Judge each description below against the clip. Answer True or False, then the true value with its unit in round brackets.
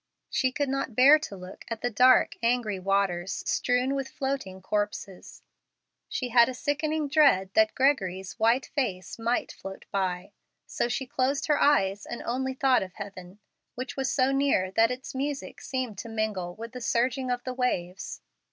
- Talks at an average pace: True (170 wpm)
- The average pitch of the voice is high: True (245 Hz)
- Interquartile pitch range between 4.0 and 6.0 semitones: True (5.3 semitones)